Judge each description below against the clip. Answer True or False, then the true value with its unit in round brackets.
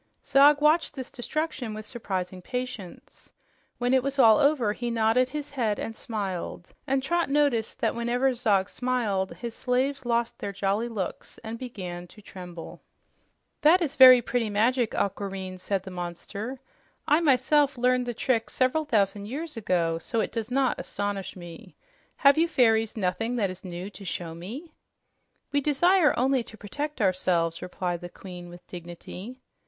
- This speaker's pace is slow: False (160 wpm)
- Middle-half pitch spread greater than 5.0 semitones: True (5.6 semitones)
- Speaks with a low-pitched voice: False (230 Hz)